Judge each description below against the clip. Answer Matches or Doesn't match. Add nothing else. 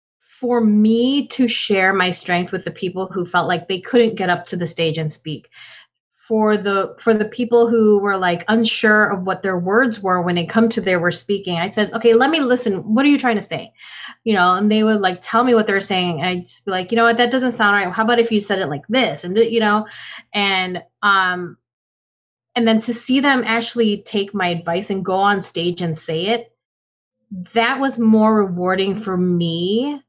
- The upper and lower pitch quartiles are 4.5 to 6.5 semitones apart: Doesn't match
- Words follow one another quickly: Matches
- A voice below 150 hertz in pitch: Doesn't match